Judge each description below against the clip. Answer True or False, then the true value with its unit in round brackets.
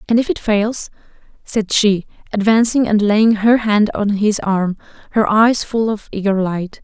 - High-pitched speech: True (210 Hz)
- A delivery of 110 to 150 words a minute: False (175 wpm)